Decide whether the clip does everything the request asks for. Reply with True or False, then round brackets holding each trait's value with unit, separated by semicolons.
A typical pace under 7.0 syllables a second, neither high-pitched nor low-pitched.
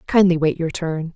True (5.0 syllables/s; 170 Hz)